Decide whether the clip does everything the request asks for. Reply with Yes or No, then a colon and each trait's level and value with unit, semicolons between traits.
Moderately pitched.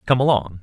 No: low, 115 Hz